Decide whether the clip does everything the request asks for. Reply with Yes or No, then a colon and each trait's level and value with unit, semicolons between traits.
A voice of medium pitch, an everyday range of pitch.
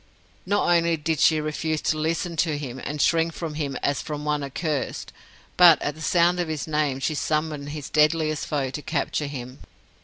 No: medium, 155 Hz; narrow, 1.9 semitones